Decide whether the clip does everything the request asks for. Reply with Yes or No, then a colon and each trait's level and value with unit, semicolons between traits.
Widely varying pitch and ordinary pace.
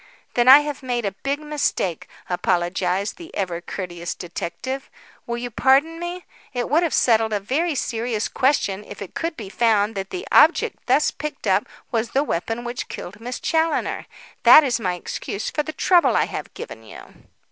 Yes: wide, 6.8 semitones; average, 180 wpm